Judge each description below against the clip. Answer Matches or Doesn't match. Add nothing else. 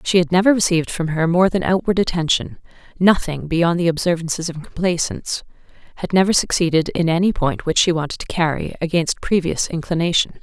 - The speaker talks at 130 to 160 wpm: Doesn't match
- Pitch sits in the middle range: Matches